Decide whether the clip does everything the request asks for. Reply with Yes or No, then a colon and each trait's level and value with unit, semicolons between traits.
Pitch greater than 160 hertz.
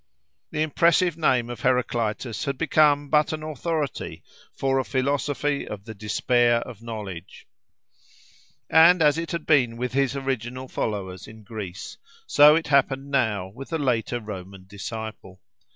No: low, 125 Hz